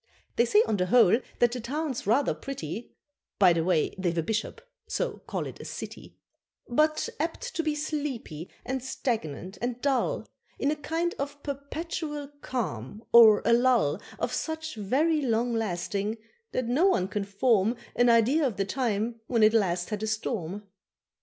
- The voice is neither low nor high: No, high, 235 Hz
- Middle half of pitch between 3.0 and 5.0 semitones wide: No, wide, 5.6 semitones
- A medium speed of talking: Yes, average, 170 wpm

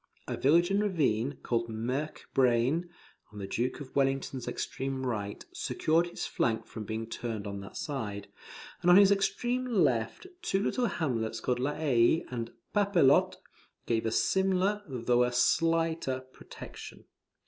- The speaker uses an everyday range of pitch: No, wide, 6.3 semitones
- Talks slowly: No, average, 150 wpm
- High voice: No, low, 130 Hz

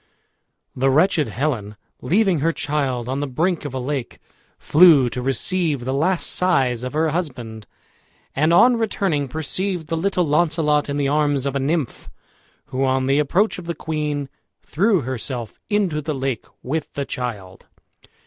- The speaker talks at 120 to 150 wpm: No, average, 160 wpm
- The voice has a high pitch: No, medium, 145 Hz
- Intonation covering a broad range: No, average, 4.1 semitones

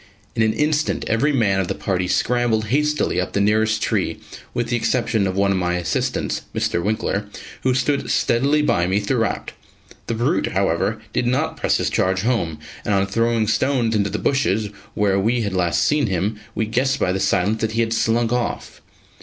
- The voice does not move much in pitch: No, average, 3.7 semitones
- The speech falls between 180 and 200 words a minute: Yes, average, 195 wpm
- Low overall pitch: Yes, low, 110 Hz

